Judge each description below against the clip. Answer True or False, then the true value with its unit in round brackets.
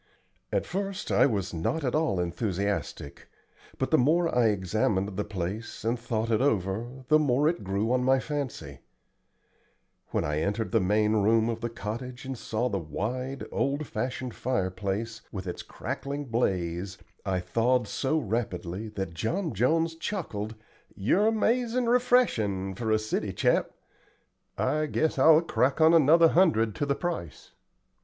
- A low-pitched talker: True (115 Hz)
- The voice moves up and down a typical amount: False (6.5 semitones)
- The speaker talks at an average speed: True (150 wpm)